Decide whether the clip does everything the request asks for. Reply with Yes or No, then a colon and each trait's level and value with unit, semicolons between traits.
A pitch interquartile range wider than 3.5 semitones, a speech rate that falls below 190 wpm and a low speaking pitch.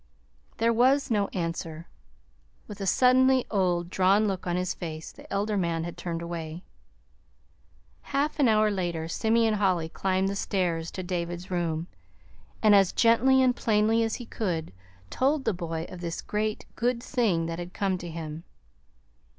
No: average, 4.6 semitones; average, 160 wpm; high, 190 Hz